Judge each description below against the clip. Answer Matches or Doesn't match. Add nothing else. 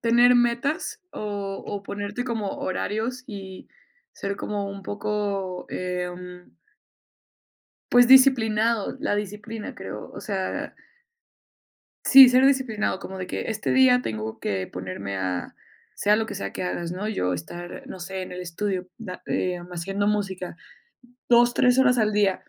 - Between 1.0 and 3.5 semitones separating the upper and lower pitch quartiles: Doesn't match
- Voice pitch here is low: Doesn't match